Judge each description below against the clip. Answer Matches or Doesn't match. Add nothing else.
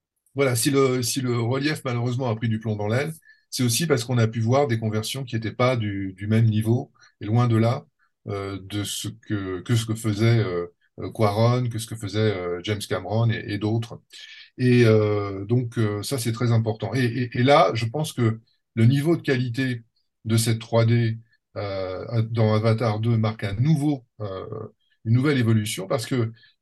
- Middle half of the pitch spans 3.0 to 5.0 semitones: Doesn't match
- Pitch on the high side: Doesn't match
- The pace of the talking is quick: Doesn't match